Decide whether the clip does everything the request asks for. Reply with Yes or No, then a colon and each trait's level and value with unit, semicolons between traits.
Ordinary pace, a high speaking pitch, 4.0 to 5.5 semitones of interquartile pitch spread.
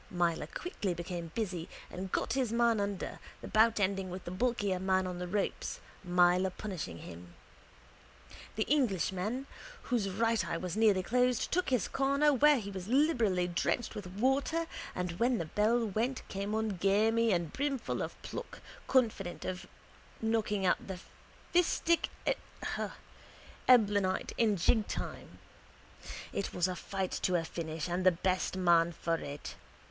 Yes: average, 150 wpm; high, 195 Hz; average, 4.4 semitones